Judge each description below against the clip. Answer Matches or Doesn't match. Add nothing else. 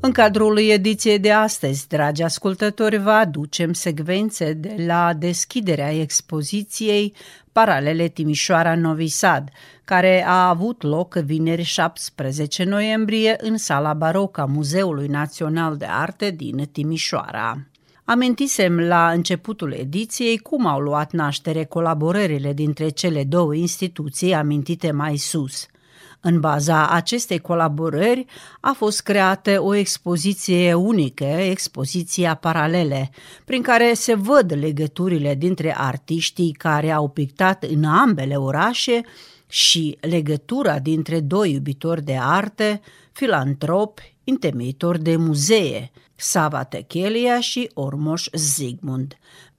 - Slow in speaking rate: Matches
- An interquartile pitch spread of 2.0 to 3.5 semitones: Doesn't match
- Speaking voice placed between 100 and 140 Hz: Doesn't match